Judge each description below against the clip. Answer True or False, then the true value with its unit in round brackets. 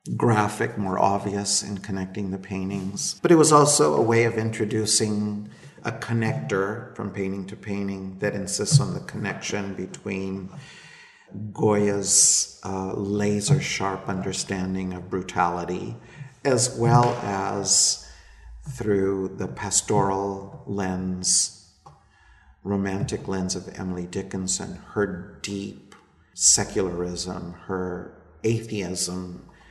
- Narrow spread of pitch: True (2.2 semitones)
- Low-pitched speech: True (100 Hz)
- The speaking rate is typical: False (105 wpm)